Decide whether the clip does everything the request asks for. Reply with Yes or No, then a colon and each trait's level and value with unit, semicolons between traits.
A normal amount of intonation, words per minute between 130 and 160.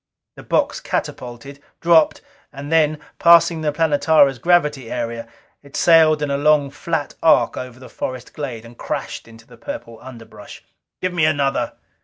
Yes: average, 4.3 semitones; average, 155 wpm